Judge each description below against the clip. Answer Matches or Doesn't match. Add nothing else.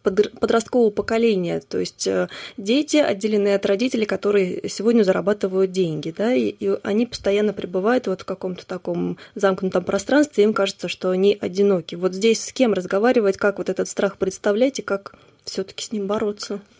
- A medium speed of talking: Doesn't match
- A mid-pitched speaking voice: Doesn't match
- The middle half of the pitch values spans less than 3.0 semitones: Matches